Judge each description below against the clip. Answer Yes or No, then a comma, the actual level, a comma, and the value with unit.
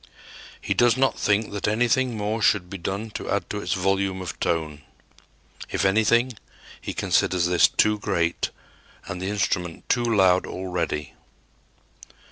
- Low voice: Yes, low, 100 Hz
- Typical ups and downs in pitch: Yes, average, 3.3 semitones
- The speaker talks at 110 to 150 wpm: Yes, average, 145 wpm